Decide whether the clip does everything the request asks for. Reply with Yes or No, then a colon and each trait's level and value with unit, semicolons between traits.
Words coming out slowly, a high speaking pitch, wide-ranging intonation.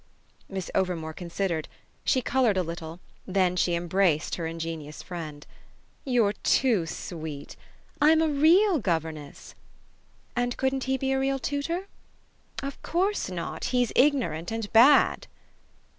Yes: slow, 130 wpm; high, 195 Hz; wide, 8.2 semitones